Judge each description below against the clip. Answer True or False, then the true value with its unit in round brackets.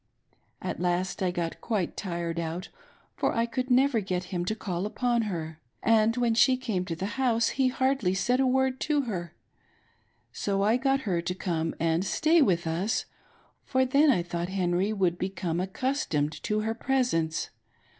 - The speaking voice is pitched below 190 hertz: False (200 Hz)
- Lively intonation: True (6.3 semitones)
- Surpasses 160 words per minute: True (175 wpm)